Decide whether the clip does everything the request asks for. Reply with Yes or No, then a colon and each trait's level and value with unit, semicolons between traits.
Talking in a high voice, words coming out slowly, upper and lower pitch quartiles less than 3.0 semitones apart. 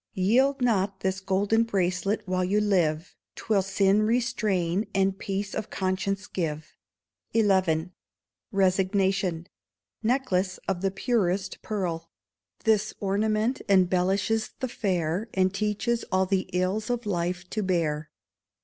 Yes: high, 195 Hz; slow, 120 wpm; narrow, 2.6 semitones